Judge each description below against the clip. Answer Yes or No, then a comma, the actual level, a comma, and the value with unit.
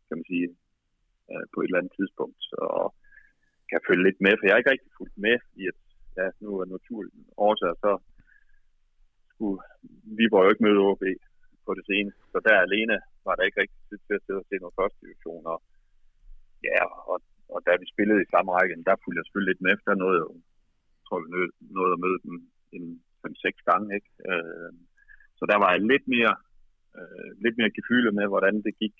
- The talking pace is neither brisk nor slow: Yes, average, 215 wpm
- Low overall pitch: Yes, low, 105 Hz